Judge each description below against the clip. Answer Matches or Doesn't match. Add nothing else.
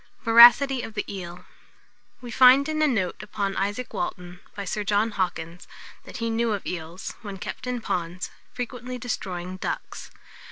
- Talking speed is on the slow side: Doesn't match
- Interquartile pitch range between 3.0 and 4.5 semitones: Doesn't match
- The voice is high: Matches